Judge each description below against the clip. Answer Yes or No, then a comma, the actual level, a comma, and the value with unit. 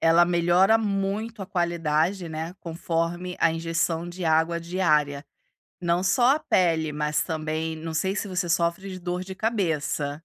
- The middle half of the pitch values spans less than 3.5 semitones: Yes, narrow, 2.5 semitones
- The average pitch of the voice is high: No, medium, 170 Hz